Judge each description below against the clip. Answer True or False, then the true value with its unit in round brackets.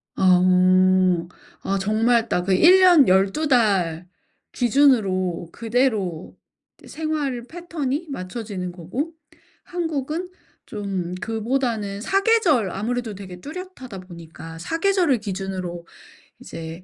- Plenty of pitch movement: True (7.6 semitones)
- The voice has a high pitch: True (225 Hz)